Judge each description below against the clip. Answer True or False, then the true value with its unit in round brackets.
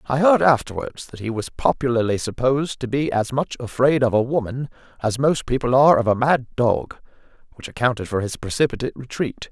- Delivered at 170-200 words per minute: True (190 wpm)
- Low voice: True (125 Hz)